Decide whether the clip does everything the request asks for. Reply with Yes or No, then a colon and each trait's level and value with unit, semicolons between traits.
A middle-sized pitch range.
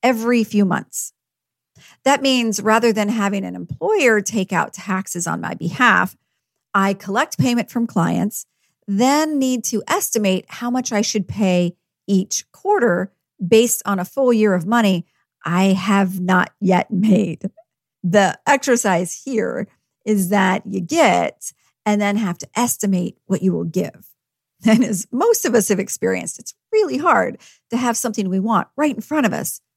Yes: average, 3.8 semitones